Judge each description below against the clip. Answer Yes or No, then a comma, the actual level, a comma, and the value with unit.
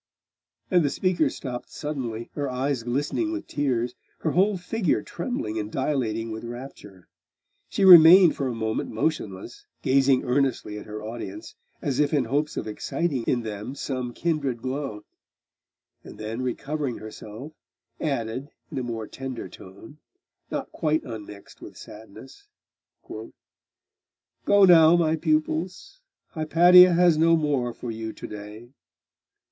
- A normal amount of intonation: No, wide, 5.7 semitones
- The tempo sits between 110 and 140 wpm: Yes, slow, 135 wpm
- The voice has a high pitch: No, low, 135 Hz